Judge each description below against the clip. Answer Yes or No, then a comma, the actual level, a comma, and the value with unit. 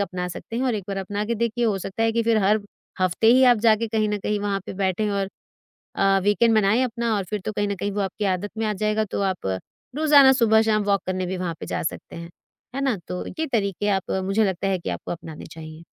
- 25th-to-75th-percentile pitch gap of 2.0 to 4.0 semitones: Yes, average, 2.8 semitones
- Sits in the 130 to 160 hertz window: No, high, 205 Hz